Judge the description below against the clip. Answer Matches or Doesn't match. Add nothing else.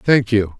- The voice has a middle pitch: Doesn't match